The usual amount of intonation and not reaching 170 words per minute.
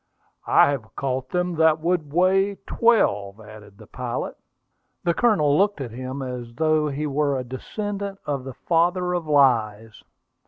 No: wide, 5.8 semitones; average, 155 wpm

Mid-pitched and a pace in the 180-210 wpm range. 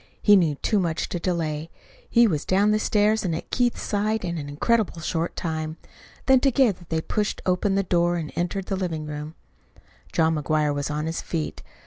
Yes: medium, 175 Hz; average, 190 wpm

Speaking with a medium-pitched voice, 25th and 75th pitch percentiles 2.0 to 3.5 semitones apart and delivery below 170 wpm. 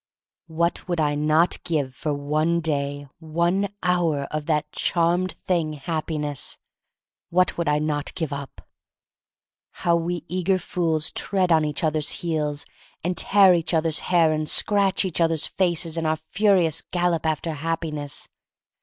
Yes: medium, 160 Hz; narrow, 2.4 semitones; average, 150 wpm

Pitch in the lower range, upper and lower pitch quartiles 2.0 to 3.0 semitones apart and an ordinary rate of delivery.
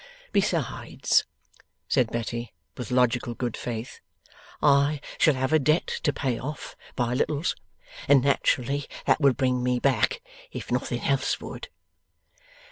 No: low, 130 Hz; average, 2.7 semitones; slow, 130 wpm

